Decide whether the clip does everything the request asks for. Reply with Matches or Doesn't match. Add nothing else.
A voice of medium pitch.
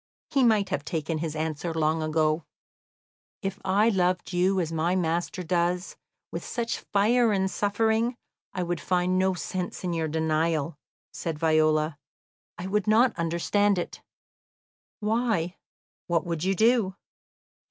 Matches